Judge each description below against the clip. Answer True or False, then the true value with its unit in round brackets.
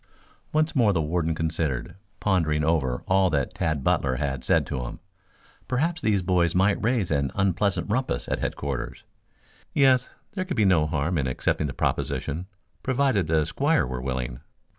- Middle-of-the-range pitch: False (85 Hz)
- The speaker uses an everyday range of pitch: False (6.7 semitones)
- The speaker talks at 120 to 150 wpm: False (160 wpm)